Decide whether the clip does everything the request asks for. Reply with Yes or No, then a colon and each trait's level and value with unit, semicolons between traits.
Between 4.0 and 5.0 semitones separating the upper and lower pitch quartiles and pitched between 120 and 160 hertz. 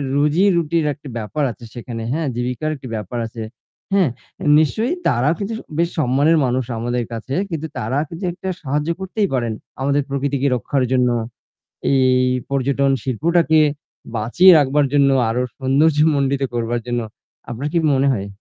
Yes: average, 4.3 semitones; medium, 140 Hz